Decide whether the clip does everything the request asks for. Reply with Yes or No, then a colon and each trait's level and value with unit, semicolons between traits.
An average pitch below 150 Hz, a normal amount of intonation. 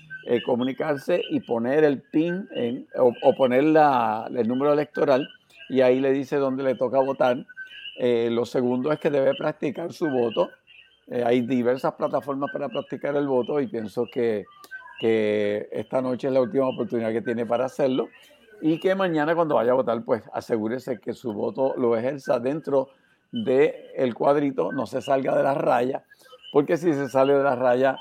Yes: low, 135 Hz; average, 4.1 semitones